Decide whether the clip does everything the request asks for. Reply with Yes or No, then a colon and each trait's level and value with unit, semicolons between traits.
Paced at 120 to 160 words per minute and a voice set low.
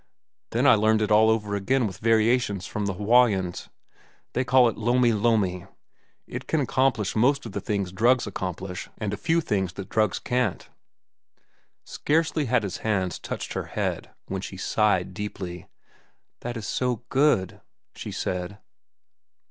Yes: average, 155 wpm; low, 105 Hz